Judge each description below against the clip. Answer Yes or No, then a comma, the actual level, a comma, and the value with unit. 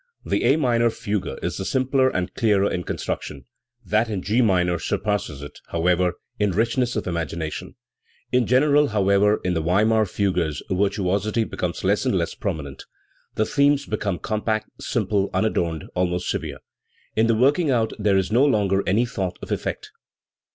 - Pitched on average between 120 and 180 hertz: No, low, 105 Hz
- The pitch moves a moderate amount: Yes, average, 4.3 semitones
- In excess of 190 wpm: No, average, 165 wpm